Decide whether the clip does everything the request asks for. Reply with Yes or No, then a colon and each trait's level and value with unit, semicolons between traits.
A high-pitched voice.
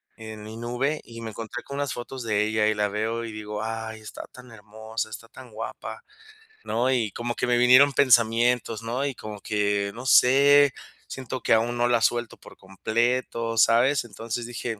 No: low, 115 Hz